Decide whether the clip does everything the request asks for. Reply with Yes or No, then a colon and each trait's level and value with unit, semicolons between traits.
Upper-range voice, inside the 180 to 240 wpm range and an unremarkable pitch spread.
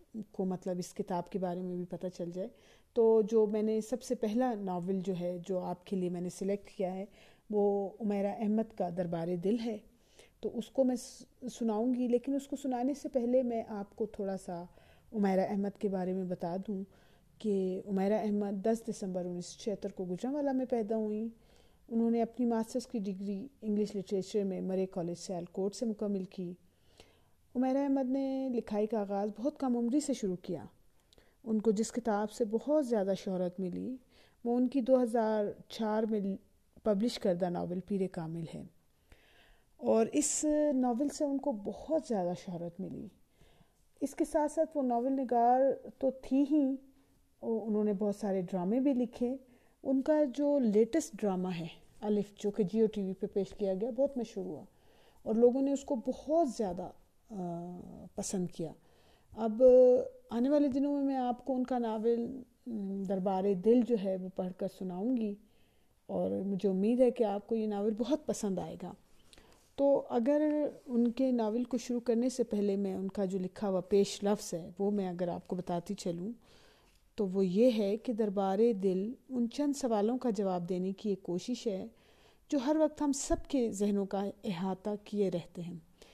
Yes: high, 215 Hz; average, 185 wpm; average, 4.4 semitones